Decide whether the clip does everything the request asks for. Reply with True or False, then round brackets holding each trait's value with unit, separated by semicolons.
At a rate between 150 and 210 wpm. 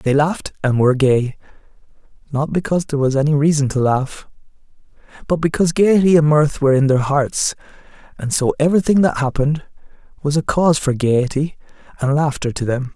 True (165 wpm)